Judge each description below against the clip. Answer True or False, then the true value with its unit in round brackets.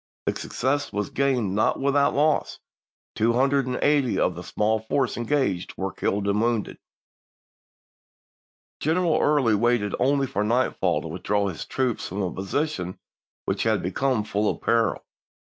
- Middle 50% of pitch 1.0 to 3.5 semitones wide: False (5.1 semitones)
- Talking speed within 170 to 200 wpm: False (155 wpm)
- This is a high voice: False (120 Hz)